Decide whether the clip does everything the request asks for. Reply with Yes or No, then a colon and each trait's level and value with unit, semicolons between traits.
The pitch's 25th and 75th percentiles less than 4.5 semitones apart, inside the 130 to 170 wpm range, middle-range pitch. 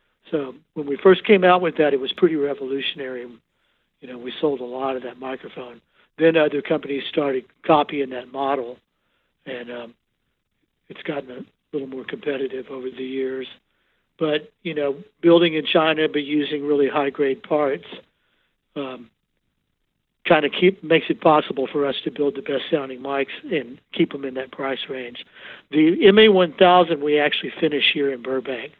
Yes: average, 3.3 semitones; average, 165 wpm; medium, 145 Hz